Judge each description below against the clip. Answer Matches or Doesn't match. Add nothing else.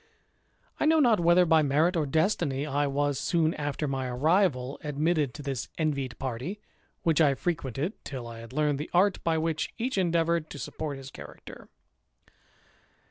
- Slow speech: Doesn't match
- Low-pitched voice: Doesn't match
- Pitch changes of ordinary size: Matches